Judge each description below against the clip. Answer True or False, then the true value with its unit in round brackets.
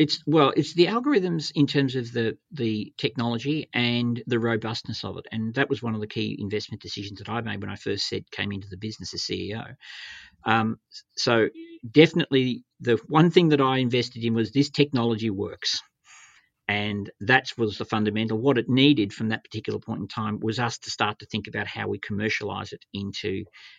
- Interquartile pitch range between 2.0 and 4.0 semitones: False (4.5 semitones)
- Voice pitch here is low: True (115 Hz)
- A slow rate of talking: False (195 wpm)